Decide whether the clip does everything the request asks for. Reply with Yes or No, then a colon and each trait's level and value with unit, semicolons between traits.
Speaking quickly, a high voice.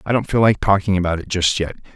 No: fast, 275 wpm; very low, 95 Hz